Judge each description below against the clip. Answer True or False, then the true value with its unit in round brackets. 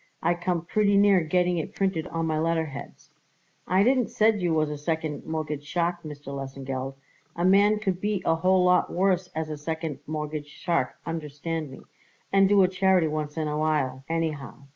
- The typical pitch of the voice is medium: True (165 Hz)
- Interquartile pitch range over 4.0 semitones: False (3.4 semitones)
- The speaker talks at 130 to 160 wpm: False (180 wpm)